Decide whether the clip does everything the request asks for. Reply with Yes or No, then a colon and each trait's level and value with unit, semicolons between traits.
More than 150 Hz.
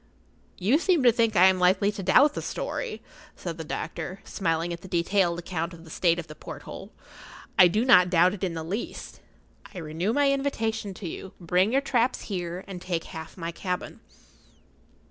Yes: medium, 185 Hz